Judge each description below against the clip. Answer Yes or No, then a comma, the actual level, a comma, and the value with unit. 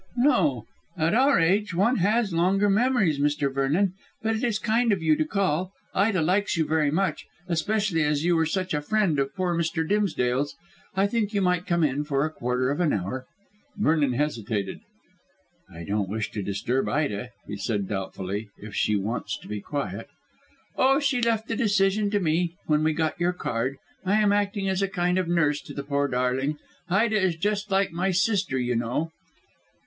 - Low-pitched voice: No, medium, 165 Hz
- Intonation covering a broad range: Yes, wide, 6.4 semitones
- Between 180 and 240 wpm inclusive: Yes, average, 190 wpm